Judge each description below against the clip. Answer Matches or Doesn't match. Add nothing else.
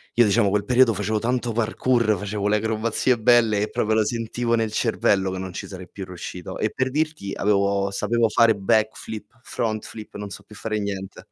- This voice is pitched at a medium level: Doesn't match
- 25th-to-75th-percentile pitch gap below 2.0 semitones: Doesn't match